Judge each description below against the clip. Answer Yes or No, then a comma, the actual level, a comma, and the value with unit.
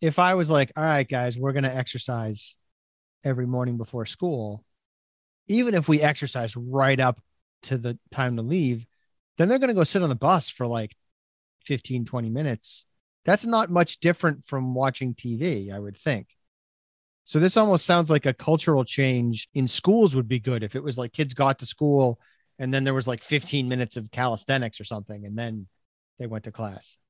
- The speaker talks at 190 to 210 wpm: Yes, average, 195 wpm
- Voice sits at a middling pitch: No, low, 125 Hz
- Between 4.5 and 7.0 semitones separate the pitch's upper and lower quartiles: Yes, average, 4.9 semitones